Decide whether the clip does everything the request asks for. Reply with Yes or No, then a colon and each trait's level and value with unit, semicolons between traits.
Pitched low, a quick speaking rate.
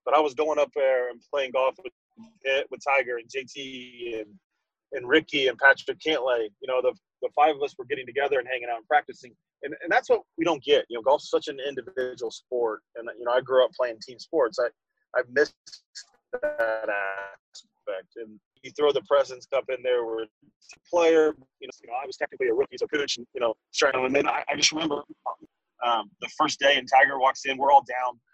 No: medium, 150 Hz; fast, 220 wpm